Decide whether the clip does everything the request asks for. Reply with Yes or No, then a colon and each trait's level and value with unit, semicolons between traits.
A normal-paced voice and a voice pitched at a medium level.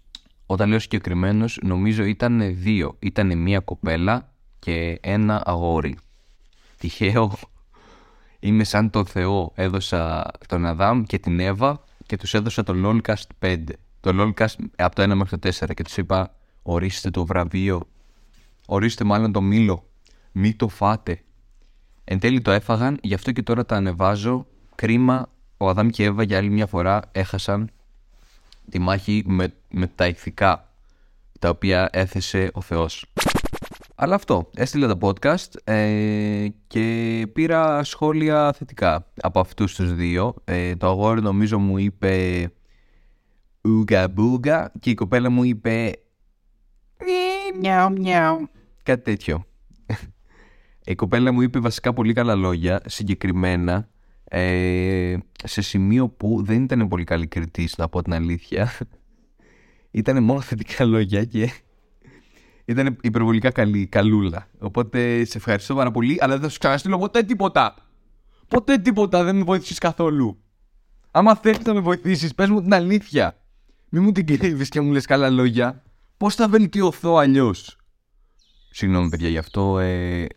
No: average, 140 wpm; low, 105 Hz